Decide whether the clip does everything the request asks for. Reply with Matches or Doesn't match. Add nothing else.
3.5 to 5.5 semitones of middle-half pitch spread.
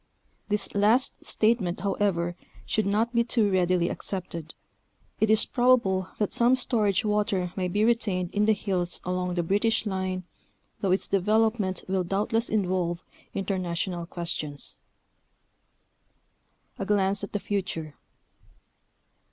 Doesn't match